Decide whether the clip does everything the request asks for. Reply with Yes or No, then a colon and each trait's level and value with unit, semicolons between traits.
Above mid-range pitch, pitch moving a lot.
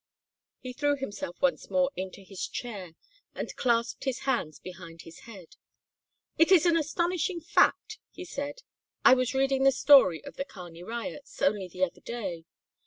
Yes: very high, 250 Hz; wide, 7.3 semitones